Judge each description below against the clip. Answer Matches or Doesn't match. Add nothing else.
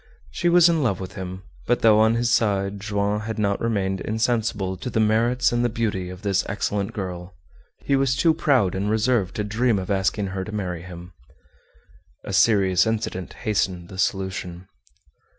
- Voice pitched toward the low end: Matches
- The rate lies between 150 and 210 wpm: Matches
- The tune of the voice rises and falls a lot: Doesn't match